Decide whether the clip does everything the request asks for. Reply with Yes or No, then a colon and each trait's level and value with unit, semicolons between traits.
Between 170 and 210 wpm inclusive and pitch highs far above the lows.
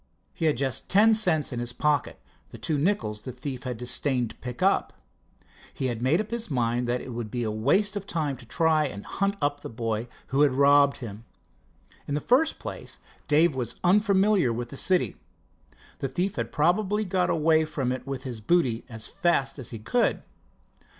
Yes: average, 195 wpm; wide, 6.5 semitones